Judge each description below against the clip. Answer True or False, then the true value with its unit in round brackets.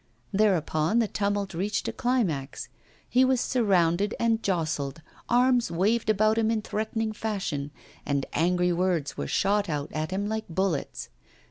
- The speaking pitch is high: True (200 Hz)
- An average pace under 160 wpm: True (145 wpm)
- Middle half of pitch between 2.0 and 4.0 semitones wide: False (5.0 semitones)